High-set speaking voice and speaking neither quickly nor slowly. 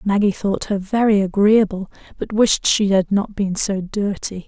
Yes: high, 200 Hz; average, 175 wpm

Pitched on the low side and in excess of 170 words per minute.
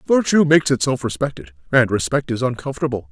No: low, 130 Hz; average, 155 wpm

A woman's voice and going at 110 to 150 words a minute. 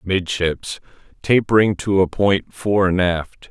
No: male; slow, 135 wpm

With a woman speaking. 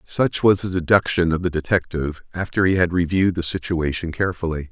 No: male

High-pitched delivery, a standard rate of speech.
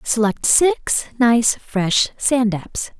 No: high, 225 Hz; slow, 120 wpm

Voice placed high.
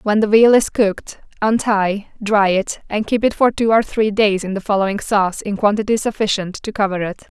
Yes: high, 210 Hz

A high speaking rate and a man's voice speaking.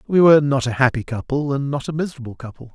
Yes: fast, 240 wpm; male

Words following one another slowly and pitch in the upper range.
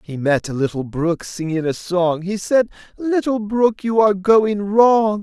No: average, 185 wpm; high, 195 Hz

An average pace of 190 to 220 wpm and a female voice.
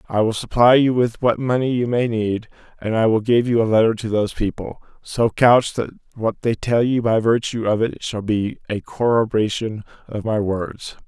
No: fast, 205 wpm; male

